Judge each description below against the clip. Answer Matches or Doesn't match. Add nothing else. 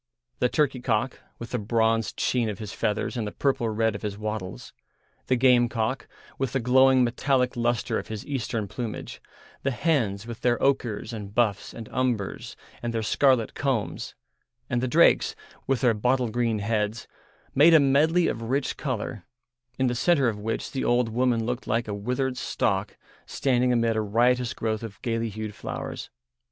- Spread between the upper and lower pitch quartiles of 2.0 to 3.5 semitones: Matches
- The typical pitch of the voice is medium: Doesn't match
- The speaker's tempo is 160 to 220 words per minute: Matches